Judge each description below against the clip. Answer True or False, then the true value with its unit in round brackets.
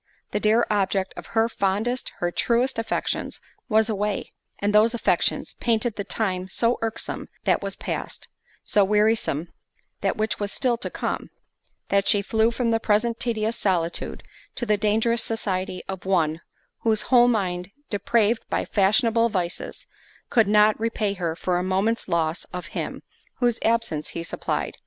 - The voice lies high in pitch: True (210 Hz)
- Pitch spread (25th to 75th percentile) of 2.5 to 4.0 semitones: True (3.3 semitones)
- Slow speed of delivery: False (155 wpm)